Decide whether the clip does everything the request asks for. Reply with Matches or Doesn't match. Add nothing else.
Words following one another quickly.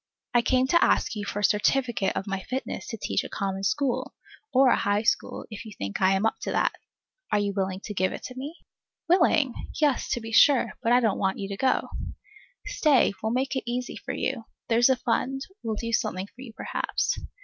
Matches